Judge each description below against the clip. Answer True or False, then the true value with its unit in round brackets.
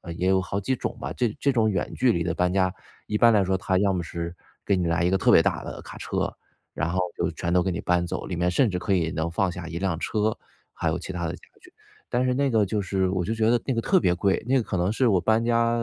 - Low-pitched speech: True (95 Hz)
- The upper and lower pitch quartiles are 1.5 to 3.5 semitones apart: False (4.0 semitones)